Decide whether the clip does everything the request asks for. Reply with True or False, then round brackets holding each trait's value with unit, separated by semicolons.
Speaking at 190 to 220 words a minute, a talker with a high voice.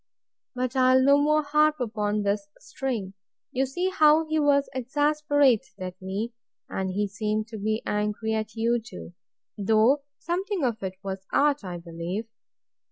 False (155 wpm; 230 Hz)